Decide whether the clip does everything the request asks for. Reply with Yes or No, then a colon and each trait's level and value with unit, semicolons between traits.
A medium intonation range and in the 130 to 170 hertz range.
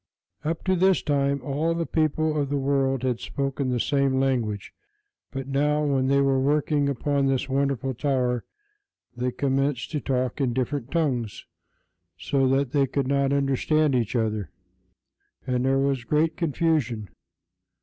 No: narrow, 2.1 semitones; low, 135 Hz